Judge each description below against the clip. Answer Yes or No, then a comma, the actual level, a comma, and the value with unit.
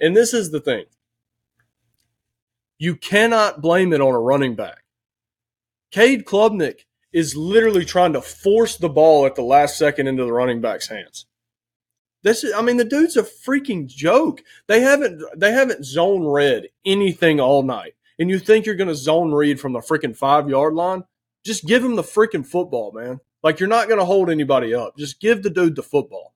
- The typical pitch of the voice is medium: Yes, medium, 160 Hz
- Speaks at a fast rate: No, average, 190 wpm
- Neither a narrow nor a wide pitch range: No, wide, 8.4 semitones